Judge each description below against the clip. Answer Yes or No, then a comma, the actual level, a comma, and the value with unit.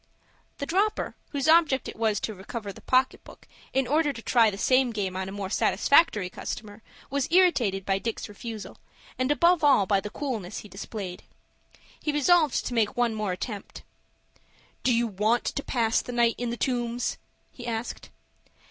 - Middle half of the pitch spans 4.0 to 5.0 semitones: Yes, average, 4.5 semitones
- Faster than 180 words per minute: No, average, 175 wpm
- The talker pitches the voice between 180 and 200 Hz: No, high, 235 Hz